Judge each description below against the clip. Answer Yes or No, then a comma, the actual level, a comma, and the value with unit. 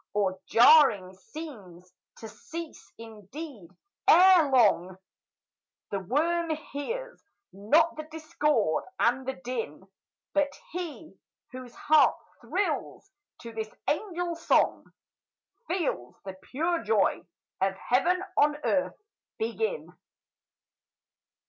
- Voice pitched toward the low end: No, very high, 275 Hz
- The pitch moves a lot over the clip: Yes, wide, 7.8 semitones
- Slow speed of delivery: Yes, slow, 100 wpm